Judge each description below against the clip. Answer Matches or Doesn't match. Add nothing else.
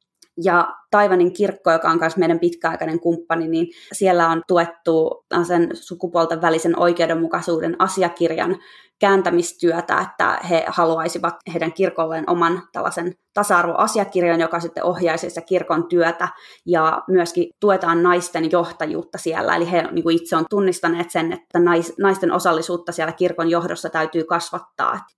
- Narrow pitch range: Matches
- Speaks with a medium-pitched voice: Matches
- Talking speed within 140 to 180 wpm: Doesn't match